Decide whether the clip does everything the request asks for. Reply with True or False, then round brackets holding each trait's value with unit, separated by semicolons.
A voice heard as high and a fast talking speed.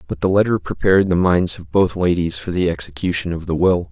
False (90 Hz; 230 wpm)